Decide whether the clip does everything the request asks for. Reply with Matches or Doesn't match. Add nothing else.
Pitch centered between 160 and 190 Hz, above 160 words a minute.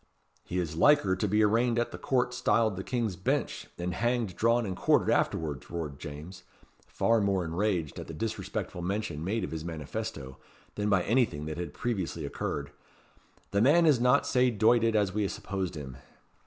Doesn't match